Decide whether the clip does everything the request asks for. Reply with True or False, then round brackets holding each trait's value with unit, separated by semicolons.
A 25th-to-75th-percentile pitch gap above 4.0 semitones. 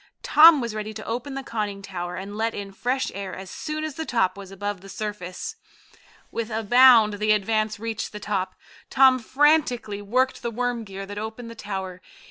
False (3.6 semitones)